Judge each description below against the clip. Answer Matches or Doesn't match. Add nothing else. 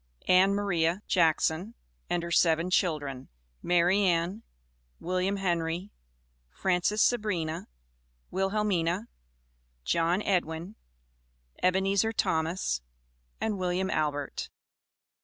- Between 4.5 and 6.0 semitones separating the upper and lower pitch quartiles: Doesn't match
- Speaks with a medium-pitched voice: Matches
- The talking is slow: Matches